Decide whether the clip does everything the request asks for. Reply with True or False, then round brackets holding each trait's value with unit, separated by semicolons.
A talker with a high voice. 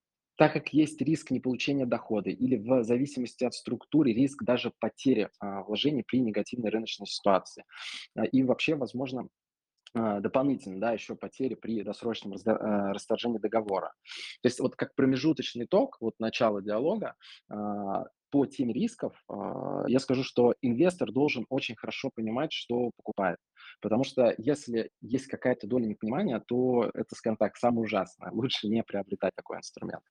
False (120 Hz)